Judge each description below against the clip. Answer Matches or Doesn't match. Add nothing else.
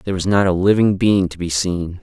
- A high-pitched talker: Doesn't match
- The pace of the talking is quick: Matches